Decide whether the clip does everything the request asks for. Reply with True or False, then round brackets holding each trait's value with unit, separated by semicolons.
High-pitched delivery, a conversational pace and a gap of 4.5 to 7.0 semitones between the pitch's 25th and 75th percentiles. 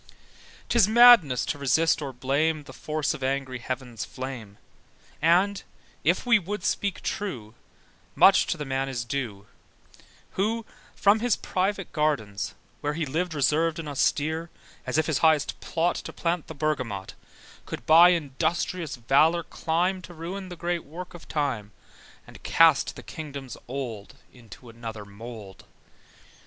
False (150 Hz; 145 wpm; 5.2 semitones)